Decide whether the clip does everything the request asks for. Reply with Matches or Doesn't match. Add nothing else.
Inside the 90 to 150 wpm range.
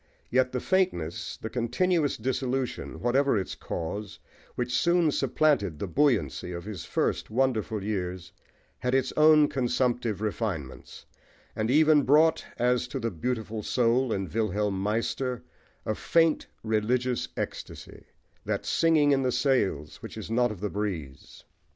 Matches